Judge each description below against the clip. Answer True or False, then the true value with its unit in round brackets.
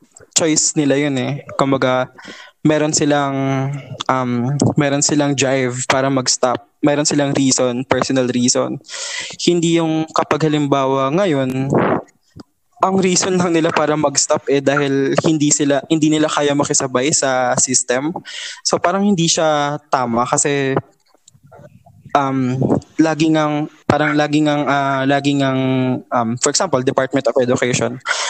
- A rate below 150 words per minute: True (130 wpm)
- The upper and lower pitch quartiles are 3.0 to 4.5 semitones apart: False (2.6 semitones)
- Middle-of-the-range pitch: True (145 Hz)